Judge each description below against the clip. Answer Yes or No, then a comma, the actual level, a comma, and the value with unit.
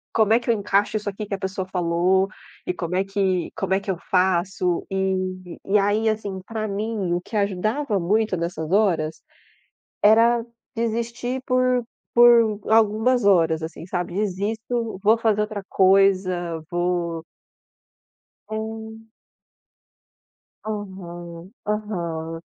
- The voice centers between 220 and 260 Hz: No, high, 195 Hz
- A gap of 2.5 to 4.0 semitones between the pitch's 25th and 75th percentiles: Yes, average, 3.4 semitones